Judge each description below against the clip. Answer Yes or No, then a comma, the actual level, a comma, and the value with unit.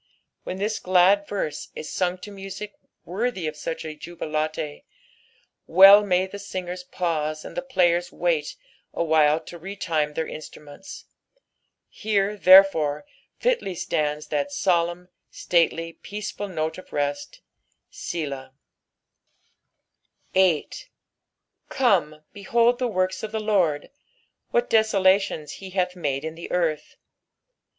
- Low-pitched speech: No, medium, 180 Hz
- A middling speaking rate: No, slow, 120 wpm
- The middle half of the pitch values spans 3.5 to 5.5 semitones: Yes, average, 4.3 semitones